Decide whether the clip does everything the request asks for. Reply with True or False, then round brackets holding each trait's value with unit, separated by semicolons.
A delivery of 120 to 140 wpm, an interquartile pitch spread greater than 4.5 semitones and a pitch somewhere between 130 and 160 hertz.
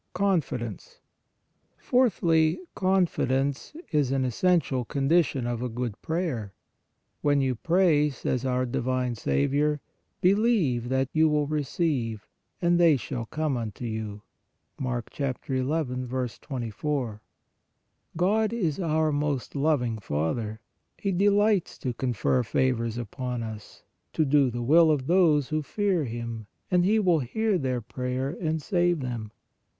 True (135 wpm; 5.2 semitones; 135 Hz)